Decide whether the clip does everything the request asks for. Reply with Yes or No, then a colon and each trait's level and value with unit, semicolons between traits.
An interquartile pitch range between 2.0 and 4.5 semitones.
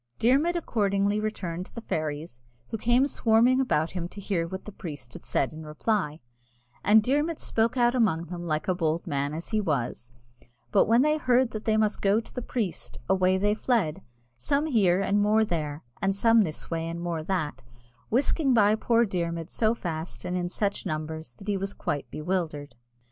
No: wide, 5.6 semitones